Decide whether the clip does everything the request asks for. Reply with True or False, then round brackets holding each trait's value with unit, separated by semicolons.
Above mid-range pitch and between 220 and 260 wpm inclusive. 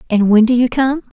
True (240 Hz; 255 wpm)